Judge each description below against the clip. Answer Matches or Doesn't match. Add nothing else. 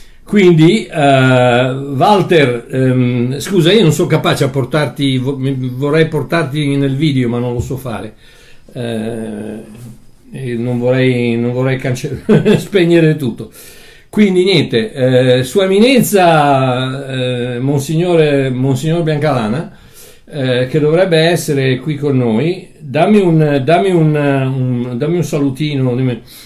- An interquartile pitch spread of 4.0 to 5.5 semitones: Matches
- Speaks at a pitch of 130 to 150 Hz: Matches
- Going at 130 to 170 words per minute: Doesn't match